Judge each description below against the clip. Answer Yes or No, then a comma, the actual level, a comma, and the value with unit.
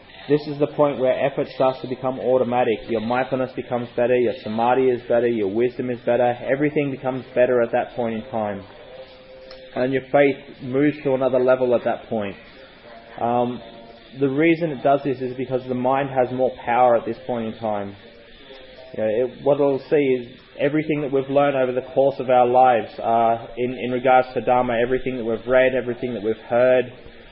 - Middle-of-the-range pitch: No, low, 125 Hz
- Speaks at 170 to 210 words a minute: Yes, average, 195 wpm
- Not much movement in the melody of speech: Yes, narrow, 1.9 semitones